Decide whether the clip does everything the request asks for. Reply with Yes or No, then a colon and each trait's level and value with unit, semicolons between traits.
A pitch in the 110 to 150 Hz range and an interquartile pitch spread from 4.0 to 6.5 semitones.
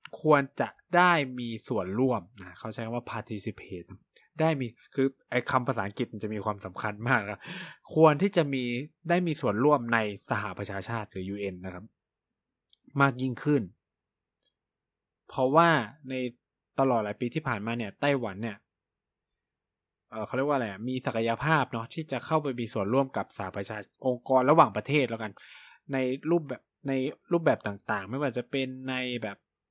Yes: low, 125 Hz; average, 4.5 semitones